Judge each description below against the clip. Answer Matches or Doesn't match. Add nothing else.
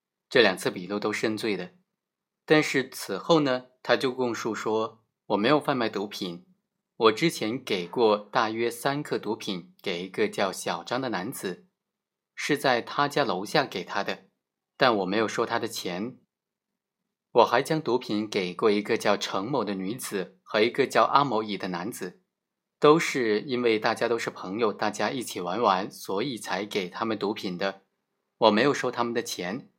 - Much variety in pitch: Matches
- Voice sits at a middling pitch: Doesn't match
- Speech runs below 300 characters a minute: Matches